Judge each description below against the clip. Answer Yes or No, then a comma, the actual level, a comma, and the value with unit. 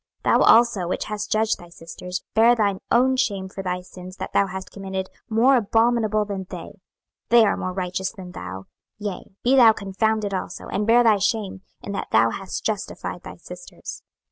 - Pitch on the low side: No, high, 200 Hz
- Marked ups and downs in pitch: No, average, 3.1 semitones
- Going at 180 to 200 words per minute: Yes, average, 190 wpm